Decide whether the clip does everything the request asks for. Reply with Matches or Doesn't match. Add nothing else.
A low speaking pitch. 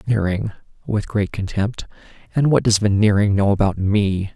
Matches